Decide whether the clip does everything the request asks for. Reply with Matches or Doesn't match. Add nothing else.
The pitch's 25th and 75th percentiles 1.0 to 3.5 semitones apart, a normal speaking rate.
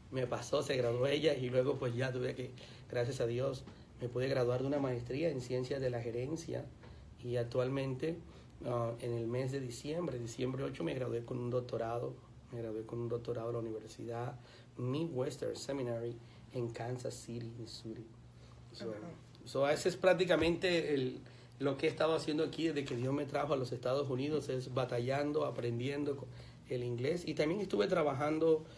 Matches